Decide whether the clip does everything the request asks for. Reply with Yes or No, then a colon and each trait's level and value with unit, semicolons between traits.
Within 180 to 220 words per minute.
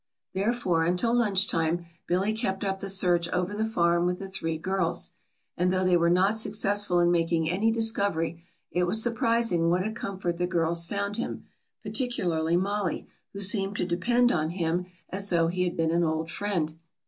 Yes: average, 185 wpm